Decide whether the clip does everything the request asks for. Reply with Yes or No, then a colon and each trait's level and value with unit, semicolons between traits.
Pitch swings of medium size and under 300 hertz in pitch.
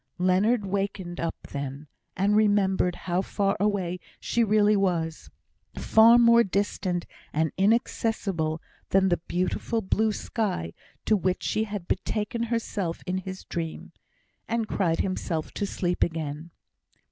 Yes: average, 3.4 semitones; high, 190 Hz